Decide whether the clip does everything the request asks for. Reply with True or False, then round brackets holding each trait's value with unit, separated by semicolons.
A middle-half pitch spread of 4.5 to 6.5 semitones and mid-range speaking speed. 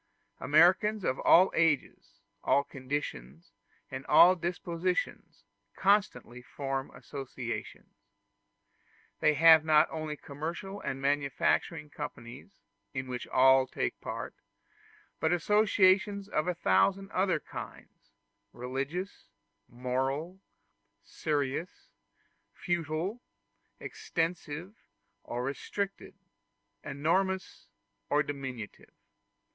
False (5.4 semitones; 85 wpm)